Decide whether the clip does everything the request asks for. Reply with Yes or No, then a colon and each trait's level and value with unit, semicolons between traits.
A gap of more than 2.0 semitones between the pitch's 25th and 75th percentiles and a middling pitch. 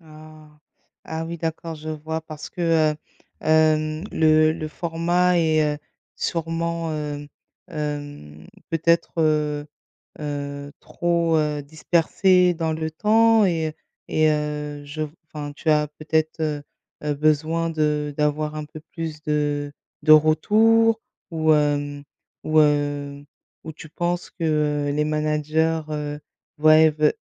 No: narrow, 1.5 semitones; medium, 155 Hz